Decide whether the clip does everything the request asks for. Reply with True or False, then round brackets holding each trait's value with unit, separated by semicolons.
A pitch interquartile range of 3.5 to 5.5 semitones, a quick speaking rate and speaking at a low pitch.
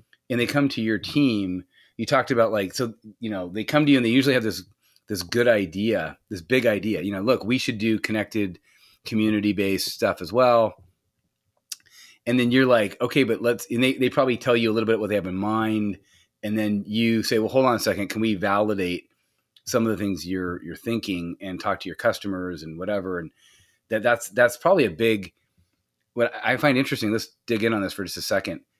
True (3.8 semitones; 225 wpm; 110 Hz)